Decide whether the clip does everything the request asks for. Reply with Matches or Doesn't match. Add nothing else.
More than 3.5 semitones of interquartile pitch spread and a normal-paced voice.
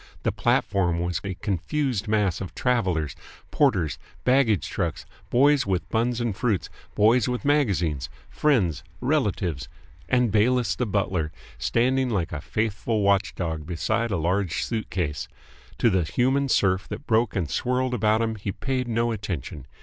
Matches